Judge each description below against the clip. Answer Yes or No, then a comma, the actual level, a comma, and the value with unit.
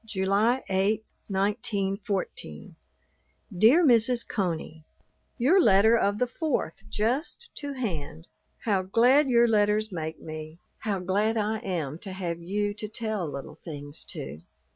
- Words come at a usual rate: No, slow, 130 wpm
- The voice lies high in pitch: Yes, high, 205 Hz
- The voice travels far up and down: No, average, 4.5 semitones